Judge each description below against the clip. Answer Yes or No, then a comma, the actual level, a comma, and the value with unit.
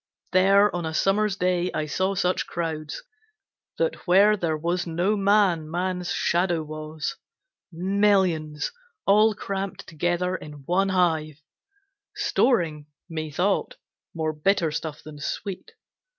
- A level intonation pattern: No, average, 3.7 semitones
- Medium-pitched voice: Yes, medium, 175 Hz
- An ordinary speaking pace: No, slow, 120 wpm